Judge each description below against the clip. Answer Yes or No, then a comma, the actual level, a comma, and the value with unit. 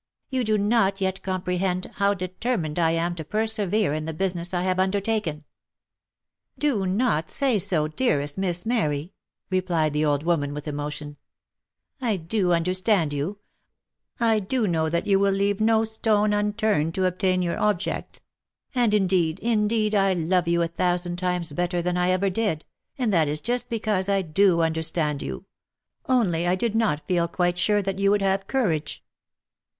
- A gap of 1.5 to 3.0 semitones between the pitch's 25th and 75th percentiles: No, average, 3.8 semitones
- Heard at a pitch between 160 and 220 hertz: Yes, medium, 185 Hz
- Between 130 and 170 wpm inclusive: No, average, 180 wpm